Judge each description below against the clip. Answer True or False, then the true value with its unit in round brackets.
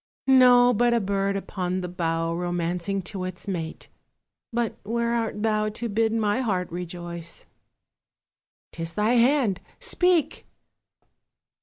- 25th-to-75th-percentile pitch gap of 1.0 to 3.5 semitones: False (4.8 semitones)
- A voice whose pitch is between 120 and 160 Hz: False (200 Hz)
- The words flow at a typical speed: False (125 wpm)